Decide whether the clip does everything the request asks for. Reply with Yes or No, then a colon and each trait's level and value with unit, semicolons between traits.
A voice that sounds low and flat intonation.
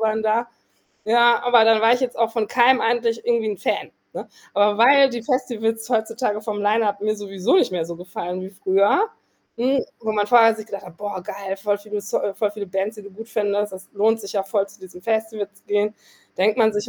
No: high, 215 Hz; narrow, 2.1 semitones